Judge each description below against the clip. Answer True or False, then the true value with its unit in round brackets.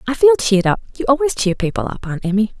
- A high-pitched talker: True (215 Hz)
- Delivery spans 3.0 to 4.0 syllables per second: False (7.2 syllables/s)